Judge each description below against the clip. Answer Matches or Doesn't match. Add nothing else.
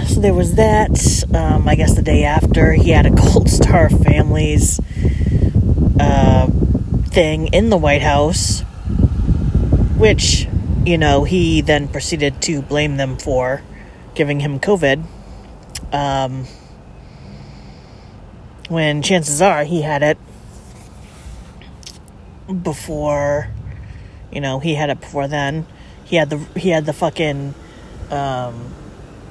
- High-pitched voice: Doesn't match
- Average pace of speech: Doesn't match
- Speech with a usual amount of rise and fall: Doesn't match